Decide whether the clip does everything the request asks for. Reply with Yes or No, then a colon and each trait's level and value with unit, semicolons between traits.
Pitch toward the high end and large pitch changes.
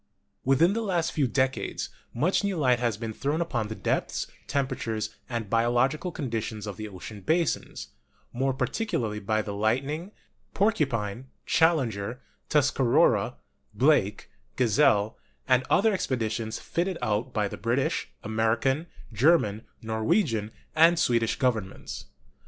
No: low, 125 Hz; wide, 5.8 semitones